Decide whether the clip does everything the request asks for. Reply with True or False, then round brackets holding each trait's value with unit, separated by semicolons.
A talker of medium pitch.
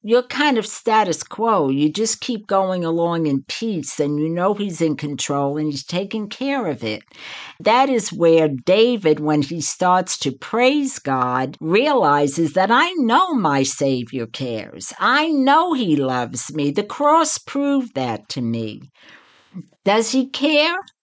True (180 Hz)